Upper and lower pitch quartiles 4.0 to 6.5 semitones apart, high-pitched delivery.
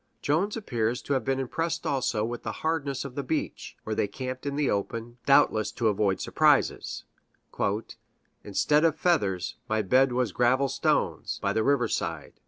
No: average, 4.5 semitones; low, 130 Hz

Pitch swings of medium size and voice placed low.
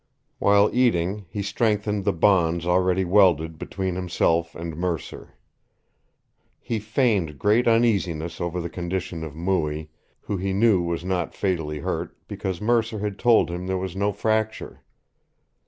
Yes: average, 3.5 semitones; very low, 95 Hz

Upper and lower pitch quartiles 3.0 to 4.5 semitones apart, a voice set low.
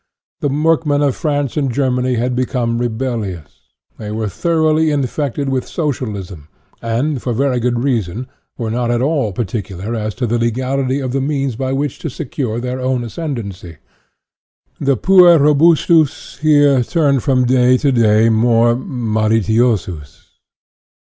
Yes: average, 3.7 semitones; low, 125 Hz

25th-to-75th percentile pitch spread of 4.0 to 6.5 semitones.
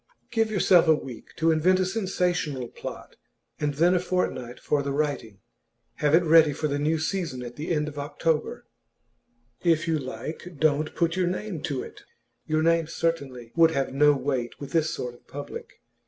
No: average, 3.1 semitones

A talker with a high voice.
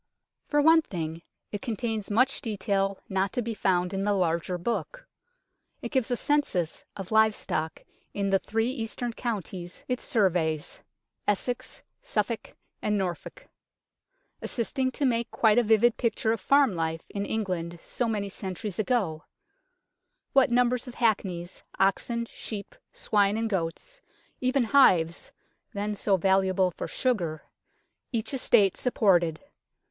Yes: high, 210 Hz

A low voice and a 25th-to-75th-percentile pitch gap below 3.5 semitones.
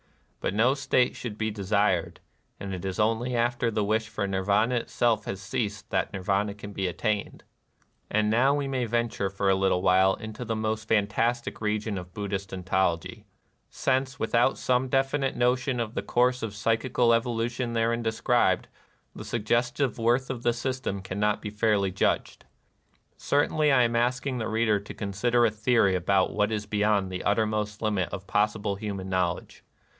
Yes: low, 110 Hz; average, 3.1 semitones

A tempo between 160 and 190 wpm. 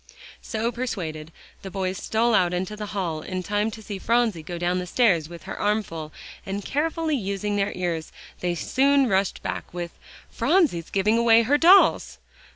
Yes: average, 175 wpm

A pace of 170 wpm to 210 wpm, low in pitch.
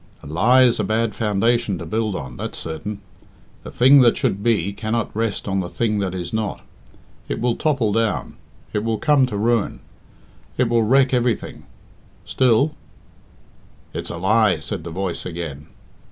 Yes: average, 175 wpm; low, 110 Hz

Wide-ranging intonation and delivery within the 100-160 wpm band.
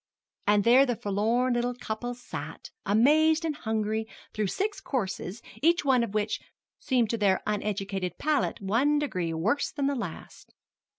No: average, 4.8 semitones; average, 155 wpm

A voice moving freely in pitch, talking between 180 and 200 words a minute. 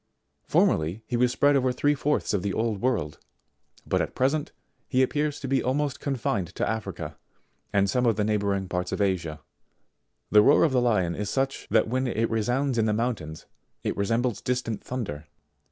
No: average, 4.5 semitones; average, 185 wpm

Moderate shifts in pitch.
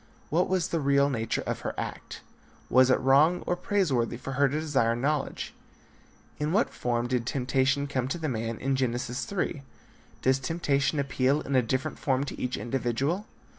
Yes: average, 3.0 semitones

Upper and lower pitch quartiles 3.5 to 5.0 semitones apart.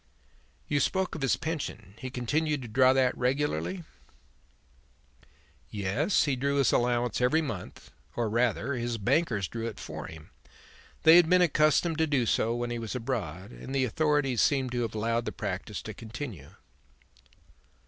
Yes: average, 4.3 semitones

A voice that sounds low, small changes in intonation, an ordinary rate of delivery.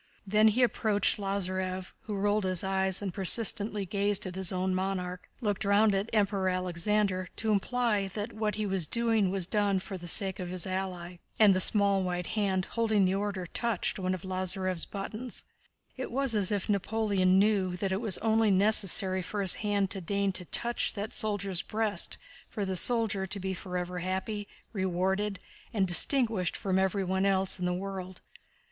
No: high, 195 Hz; narrow, 2.1 semitones; average, 180 wpm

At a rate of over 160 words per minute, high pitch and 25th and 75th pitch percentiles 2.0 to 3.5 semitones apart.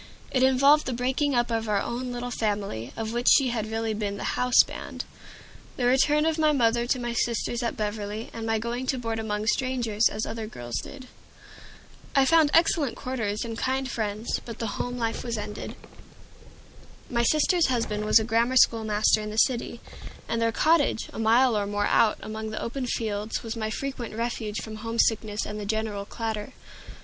Yes: average, 190 wpm; high, 230 Hz; average, 2.7 semitones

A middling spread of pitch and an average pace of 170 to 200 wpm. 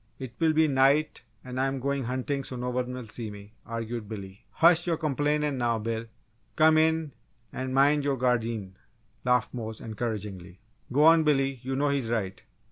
Yes: average, 4.2 semitones; average, 175 wpm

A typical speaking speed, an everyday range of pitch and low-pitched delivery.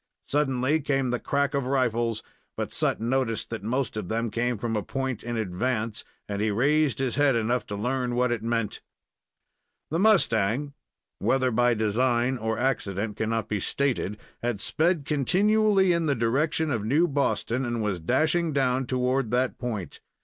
Yes: average, 165 wpm; average, 3.7 semitones; low, 125 Hz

